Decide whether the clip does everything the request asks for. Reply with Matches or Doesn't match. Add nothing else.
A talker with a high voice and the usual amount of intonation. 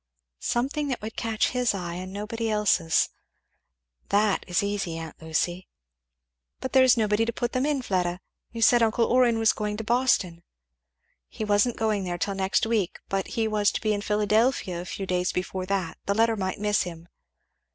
Matches